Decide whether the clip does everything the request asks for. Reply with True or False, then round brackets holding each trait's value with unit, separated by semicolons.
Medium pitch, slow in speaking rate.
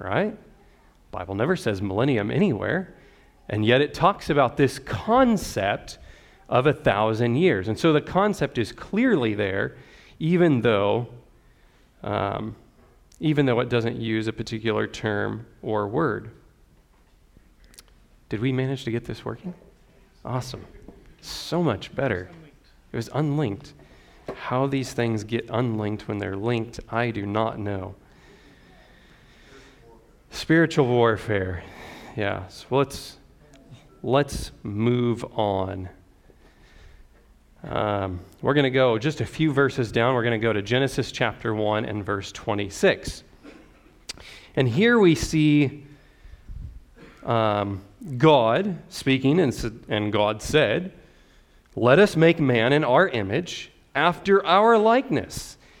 False (115 Hz; 120 wpm)